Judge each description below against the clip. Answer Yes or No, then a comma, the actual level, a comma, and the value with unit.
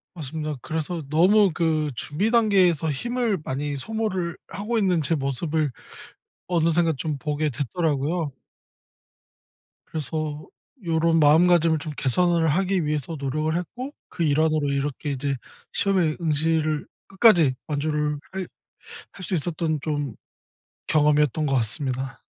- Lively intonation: No, average, 3.0 semitones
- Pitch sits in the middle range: Yes, medium, 155 Hz